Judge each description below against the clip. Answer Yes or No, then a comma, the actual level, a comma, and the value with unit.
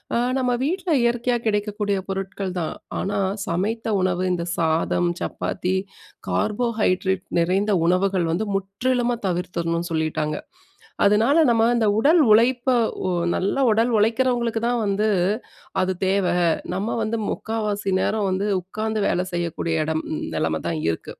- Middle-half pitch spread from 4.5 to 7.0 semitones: No, average, 4.1 semitones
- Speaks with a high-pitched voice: Yes, high, 200 Hz